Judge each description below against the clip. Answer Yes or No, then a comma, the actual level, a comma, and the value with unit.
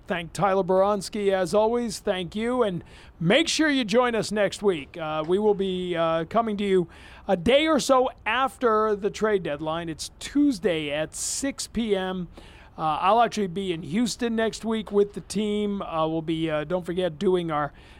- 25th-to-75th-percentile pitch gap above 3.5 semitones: Yes, average, 4.1 semitones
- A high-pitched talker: Yes, high, 200 Hz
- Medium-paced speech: Yes, average, 185 wpm